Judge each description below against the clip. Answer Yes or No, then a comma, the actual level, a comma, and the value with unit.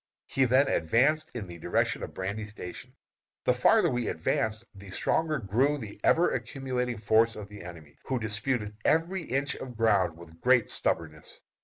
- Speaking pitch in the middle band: No, low, 110 Hz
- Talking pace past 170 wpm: No, average, 165 wpm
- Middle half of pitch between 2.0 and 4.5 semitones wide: No, average, 5.2 semitones